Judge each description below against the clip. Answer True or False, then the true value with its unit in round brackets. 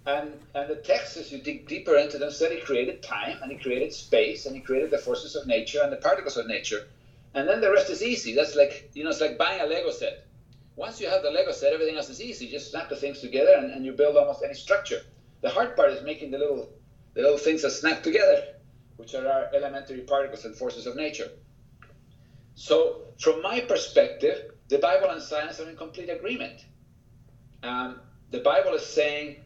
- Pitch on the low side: False (150 Hz)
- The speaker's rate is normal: False (220 wpm)